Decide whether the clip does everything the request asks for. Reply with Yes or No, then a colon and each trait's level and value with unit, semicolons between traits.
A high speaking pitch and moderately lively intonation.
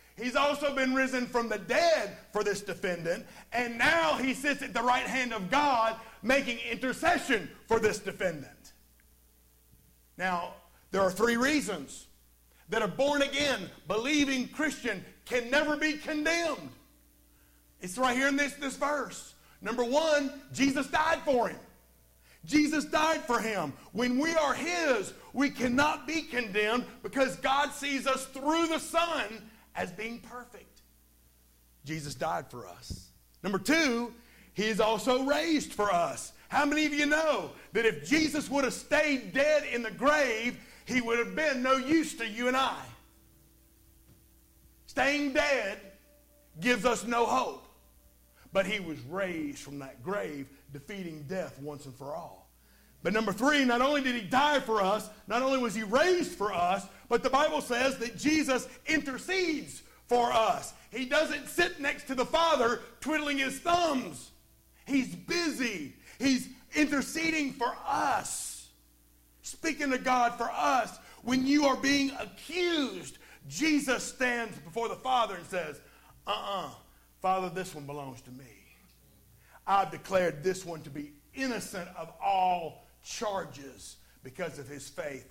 No: high, 245 Hz; wide, 7.6 semitones